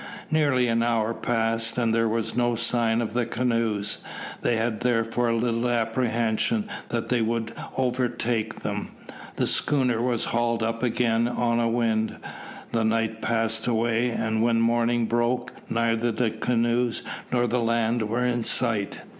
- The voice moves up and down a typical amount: No, narrow, 1.1 semitones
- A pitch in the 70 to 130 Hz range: Yes, low, 115 Hz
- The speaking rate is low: No, average, 150 wpm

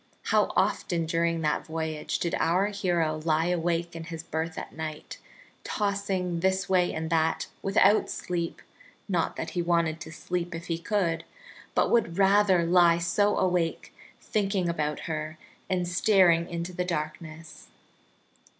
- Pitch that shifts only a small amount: Yes, narrow, 2.1 semitones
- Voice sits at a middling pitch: Yes, medium, 170 Hz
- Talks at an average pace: Yes, average, 145 wpm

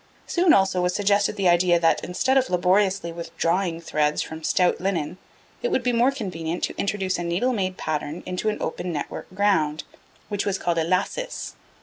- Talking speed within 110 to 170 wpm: No, average, 185 wpm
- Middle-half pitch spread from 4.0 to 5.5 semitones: No, average, 3.3 semitones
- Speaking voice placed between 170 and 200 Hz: Yes, medium, 185 Hz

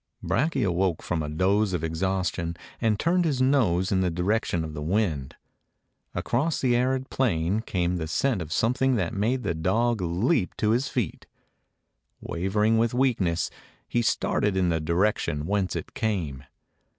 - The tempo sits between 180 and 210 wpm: No, average, 160 wpm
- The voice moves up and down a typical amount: No, wide, 5.8 semitones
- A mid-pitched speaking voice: No, low, 100 Hz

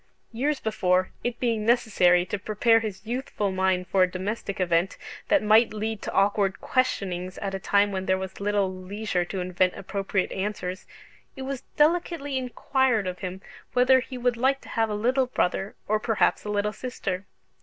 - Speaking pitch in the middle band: No, high, 205 Hz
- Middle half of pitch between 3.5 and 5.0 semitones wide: Yes, average, 4.3 semitones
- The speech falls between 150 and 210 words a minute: Yes, average, 175 wpm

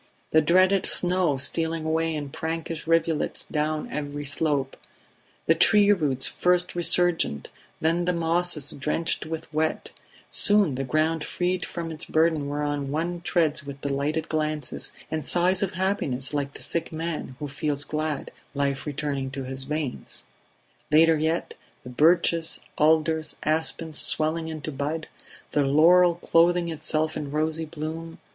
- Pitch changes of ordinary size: No, narrow, 2.3 semitones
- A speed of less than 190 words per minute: Yes, average, 140 wpm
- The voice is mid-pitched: Yes, medium, 155 Hz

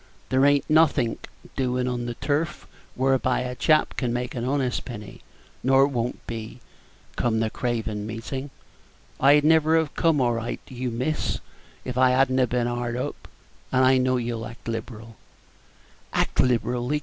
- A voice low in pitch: Yes, low, 125 Hz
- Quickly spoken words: No, average, 155 wpm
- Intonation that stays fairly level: Yes, narrow, 2.2 semitones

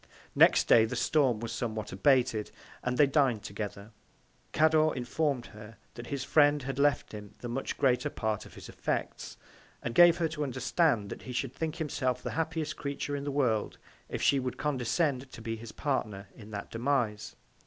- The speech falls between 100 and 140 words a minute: No, average, 185 wpm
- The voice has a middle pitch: No, low, 130 Hz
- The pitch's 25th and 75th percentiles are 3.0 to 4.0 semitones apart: No, average, 4.4 semitones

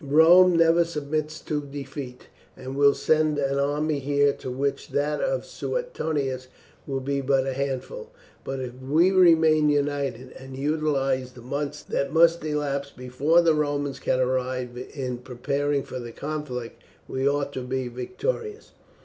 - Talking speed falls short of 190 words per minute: Yes, average, 150 wpm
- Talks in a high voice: No, medium, 140 Hz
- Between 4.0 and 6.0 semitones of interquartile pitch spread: No, average, 2.8 semitones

